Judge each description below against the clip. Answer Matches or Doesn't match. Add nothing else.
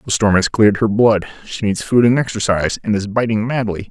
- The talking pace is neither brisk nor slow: Doesn't match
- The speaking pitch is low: Matches